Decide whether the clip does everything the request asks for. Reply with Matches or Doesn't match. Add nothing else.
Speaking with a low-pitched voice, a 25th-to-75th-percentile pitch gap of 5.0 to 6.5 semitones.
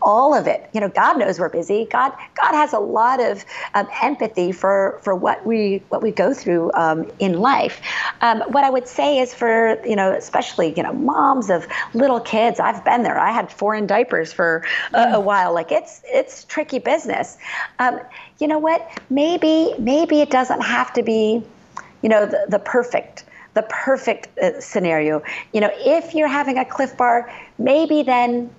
Doesn't match